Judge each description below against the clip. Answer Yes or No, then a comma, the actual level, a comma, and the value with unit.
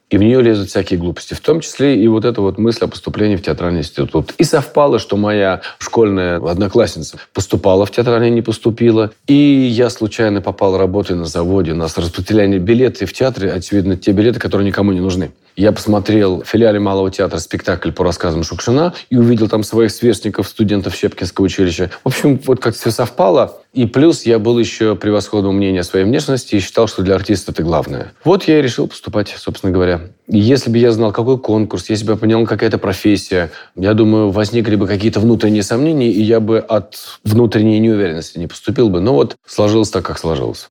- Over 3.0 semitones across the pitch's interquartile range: Yes, average, 3.4 semitones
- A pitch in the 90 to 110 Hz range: Yes, low, 105 Hz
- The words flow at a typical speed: No, fast, 200 wpm